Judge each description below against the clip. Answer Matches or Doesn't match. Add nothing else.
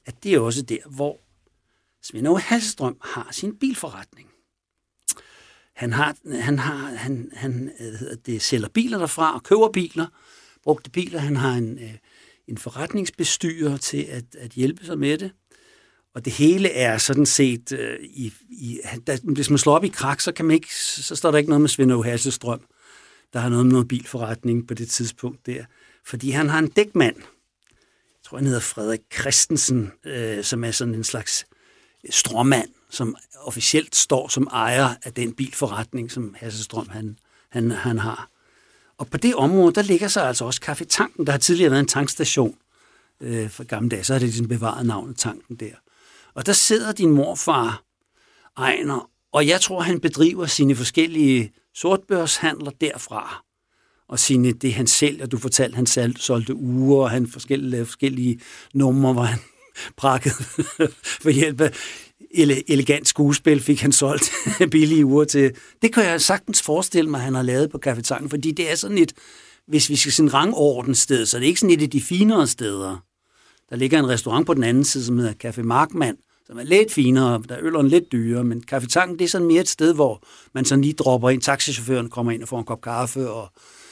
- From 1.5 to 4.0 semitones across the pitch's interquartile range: Doesn't match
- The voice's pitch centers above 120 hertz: Matches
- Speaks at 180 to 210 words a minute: Matches